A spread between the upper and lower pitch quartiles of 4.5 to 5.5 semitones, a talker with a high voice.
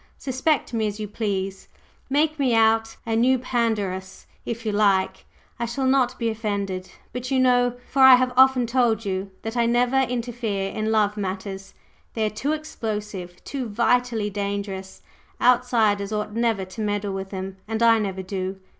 No: average, 3.6 semitones; high, 220 Hz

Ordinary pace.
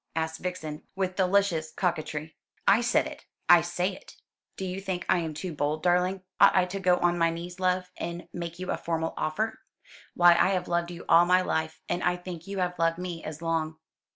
No: fast, 210 wpm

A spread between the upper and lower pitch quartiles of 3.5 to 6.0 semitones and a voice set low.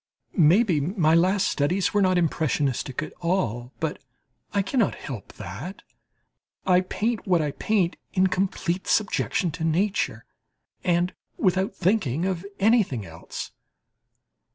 No: average, 3.9 semitones; medium, 180 Hz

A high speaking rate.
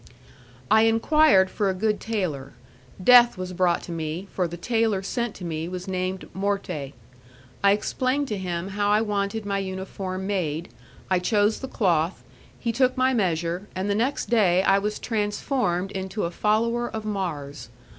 No: average, 165 wpm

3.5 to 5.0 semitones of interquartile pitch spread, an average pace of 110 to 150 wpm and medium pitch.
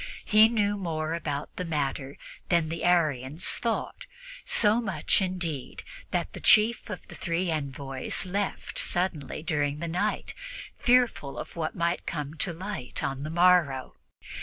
Yes: average, 4.6 semitones; average, 145 wpm; medium, 170 Hz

